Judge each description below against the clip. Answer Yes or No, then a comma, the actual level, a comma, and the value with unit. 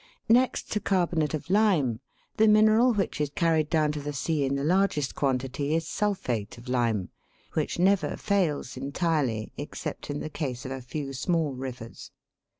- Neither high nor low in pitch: Yes, medium, 150 Hz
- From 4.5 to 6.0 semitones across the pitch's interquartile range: Yes, average, 5.3 semitones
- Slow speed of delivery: No, average, 165 wpm